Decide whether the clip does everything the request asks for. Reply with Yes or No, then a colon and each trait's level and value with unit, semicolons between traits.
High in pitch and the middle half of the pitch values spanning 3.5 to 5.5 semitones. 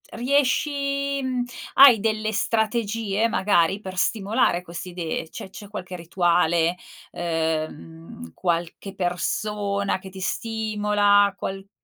Yes: high, 200 Hz; average, 4.1 semitones